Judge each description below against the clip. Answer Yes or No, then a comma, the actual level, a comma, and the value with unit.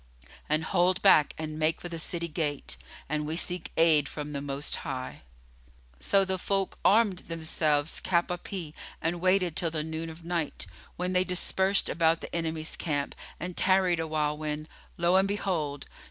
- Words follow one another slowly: No, average, 170 wpm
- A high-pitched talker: No, medium, 165 Hz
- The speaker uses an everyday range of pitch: Yes, average, 3.0 semitones